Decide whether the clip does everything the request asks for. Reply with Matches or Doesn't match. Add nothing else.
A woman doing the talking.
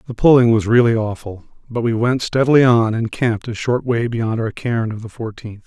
Doesn't match